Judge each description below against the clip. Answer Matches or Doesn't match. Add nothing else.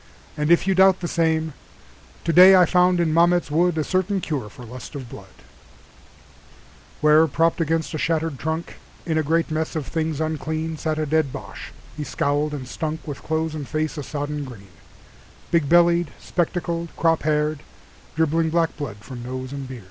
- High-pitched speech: Doesn't match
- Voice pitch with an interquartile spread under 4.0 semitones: Matches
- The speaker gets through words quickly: Doesn't match